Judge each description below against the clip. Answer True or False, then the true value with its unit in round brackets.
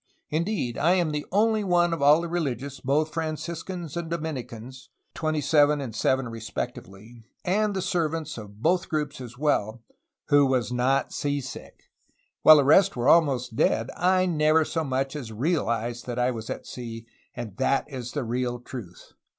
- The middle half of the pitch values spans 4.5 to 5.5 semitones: True (5.0 semitones)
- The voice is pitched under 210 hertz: True (140 Hz)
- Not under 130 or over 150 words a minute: False (160 wpm)